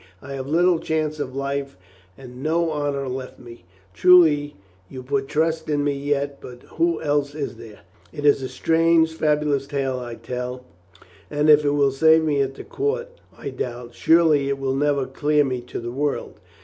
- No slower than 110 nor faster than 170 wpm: No, average, 190 wpm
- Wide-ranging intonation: No, average, 2.7 semitones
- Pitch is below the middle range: No, medium, 145 Hz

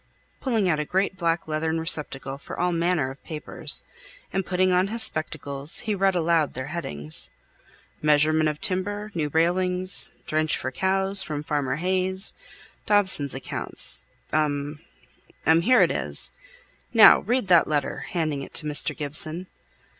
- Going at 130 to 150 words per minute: Yes, average, 145 wpm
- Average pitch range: Yes, average, 3.8 semitones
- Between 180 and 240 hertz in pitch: No, medium, 165 Hz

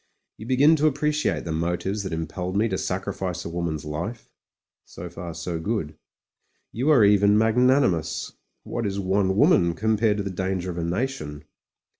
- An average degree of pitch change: Yes, average, 4.7 semitones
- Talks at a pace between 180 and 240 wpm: Yes, average, 185 wpm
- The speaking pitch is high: No, very low, 95 Hz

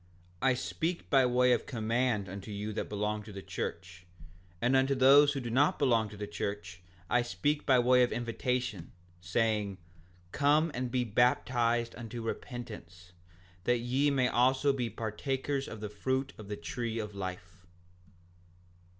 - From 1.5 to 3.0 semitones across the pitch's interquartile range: No, average, 3.9 semitones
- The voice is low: Yes, low, 120 Hz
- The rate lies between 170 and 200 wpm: No, average, 160 wpm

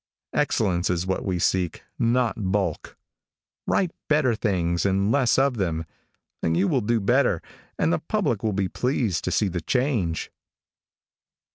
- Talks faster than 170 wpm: No, average, 150 wpm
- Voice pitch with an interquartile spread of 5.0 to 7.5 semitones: Yes, wide, 5.6 semitones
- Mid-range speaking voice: No, low, 100 Hz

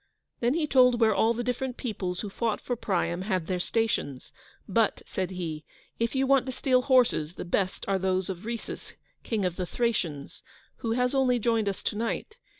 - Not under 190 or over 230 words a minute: Yes, average, 195 wpm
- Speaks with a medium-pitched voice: No, high, 225 Hz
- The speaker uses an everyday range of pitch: Yes, average, 5.0 semitones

